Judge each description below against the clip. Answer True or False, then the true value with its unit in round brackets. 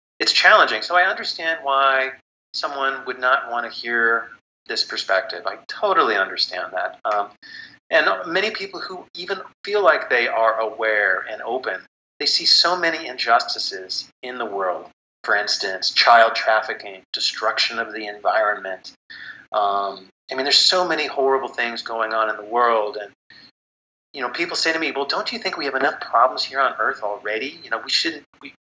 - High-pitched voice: False (115 Hz)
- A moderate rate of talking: True (170 wpm)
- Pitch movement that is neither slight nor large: True (4.5 semitones)